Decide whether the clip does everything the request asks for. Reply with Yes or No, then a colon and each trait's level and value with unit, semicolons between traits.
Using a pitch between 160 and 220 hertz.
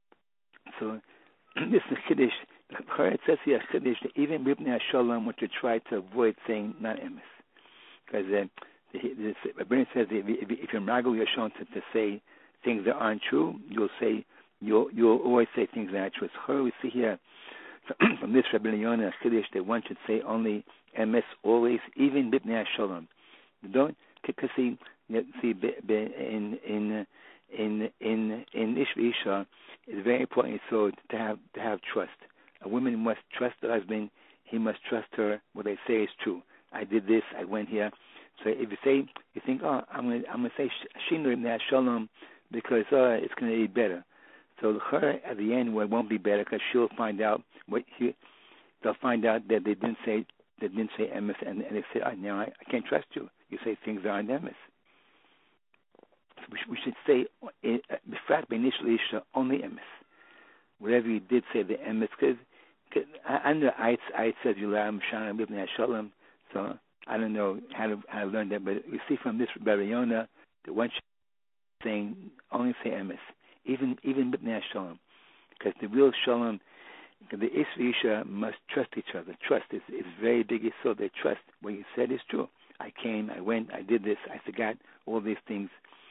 No: low, 110 Hz